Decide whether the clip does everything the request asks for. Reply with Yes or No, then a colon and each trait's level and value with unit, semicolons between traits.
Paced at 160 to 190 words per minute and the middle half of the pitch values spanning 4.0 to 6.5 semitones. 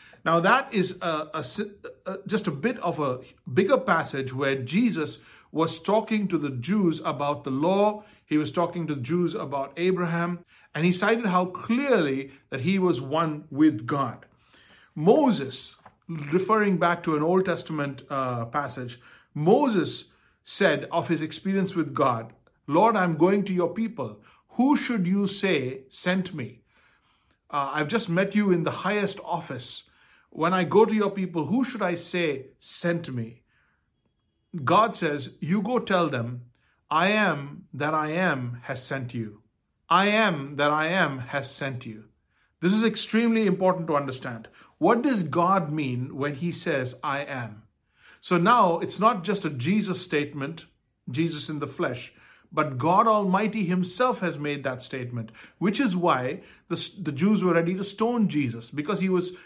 Yes: average, 165 wpm; average, 5.3 semitones